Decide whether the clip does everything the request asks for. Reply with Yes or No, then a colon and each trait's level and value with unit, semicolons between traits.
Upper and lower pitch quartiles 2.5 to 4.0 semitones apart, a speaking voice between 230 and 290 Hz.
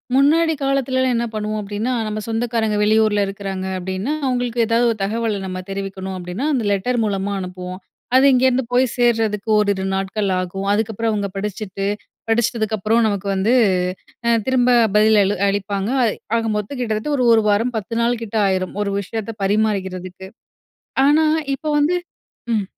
No: average, 3.3 semitones; high, 215 Hz